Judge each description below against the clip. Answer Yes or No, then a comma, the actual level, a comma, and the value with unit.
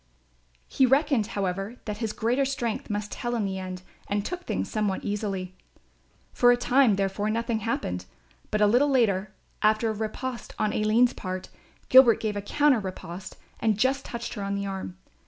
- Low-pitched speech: No, high, 215 Hz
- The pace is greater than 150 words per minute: Yes, average, 175 wpm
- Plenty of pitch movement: No, average, 3.5 semitones